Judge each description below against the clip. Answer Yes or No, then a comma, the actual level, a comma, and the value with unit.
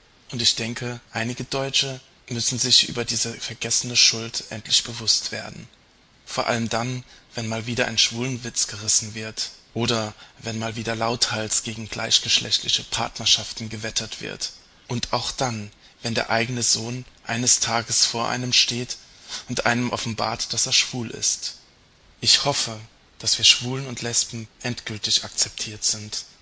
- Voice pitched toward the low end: Yes, low, 115 Hz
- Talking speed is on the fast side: No, average, 145 wpm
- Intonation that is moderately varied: No, narrow, 1.6 semitones